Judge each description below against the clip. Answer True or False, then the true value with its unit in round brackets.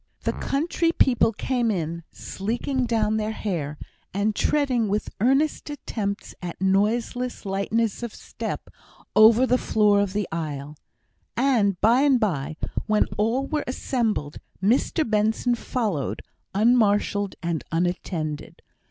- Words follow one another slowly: True (125 wpm)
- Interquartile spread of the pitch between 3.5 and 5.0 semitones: True (4.2 semitones)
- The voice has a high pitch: True (215 Hz)